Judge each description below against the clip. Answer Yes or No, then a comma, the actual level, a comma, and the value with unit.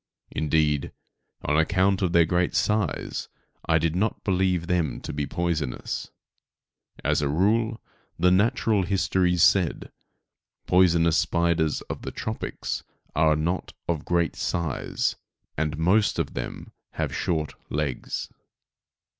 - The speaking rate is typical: No, slow, 120 wpm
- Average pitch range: Yes, average, 3.0 semitones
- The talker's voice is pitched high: No, very low, 85 Hz